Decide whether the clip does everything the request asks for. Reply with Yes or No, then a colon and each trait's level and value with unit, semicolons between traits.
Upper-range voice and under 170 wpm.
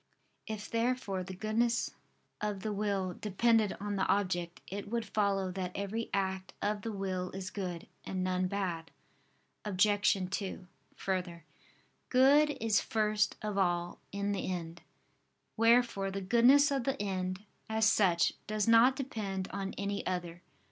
Yes: high, 200 Hz; average, 145 wpm